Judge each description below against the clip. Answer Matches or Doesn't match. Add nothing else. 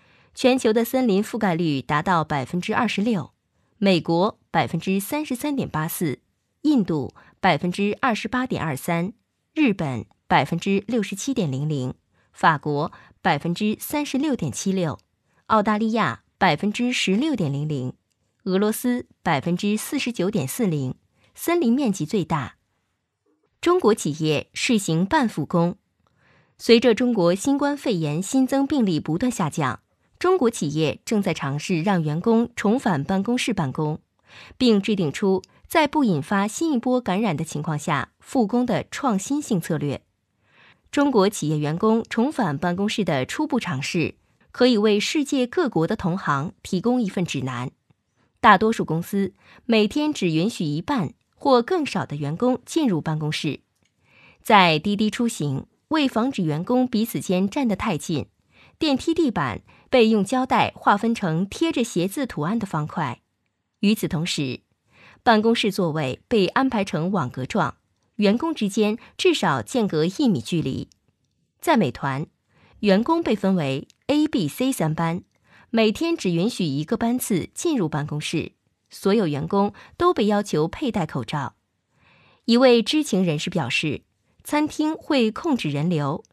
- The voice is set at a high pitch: Matches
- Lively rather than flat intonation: Matches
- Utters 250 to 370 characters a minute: Doesn't match